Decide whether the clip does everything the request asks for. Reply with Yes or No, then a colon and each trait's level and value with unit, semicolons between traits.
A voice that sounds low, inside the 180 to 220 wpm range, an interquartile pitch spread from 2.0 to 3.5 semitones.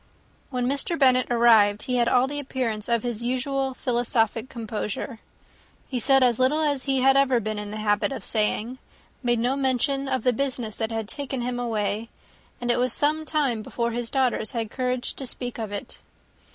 No: high, 245 Hz; average, 190 wpm; average, 2.9 semitones